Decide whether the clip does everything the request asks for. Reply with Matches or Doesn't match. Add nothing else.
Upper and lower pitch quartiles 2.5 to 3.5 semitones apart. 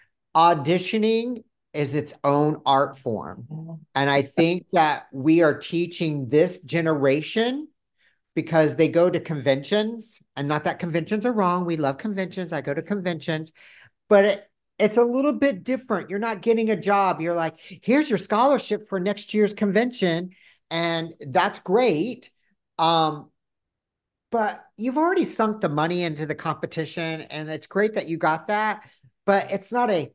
Doesn't match